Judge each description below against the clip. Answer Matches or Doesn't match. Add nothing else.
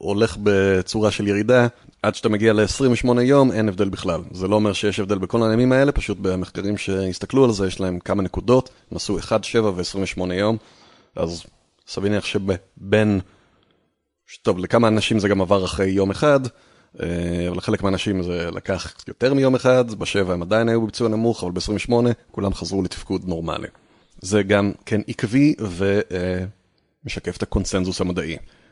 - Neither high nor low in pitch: Doesn't match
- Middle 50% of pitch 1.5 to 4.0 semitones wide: Matches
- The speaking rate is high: Matches